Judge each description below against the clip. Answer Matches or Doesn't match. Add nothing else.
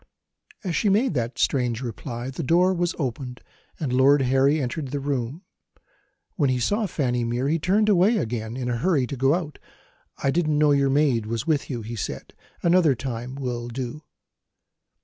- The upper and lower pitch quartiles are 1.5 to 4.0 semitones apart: Doesn't match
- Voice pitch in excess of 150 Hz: Doesn't match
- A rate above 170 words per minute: Matches